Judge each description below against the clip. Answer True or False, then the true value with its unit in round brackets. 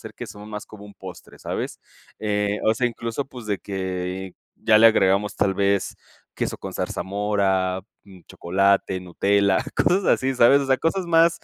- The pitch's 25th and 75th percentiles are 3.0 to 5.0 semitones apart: True (3.6 semitones)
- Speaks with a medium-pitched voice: False (100 Hz)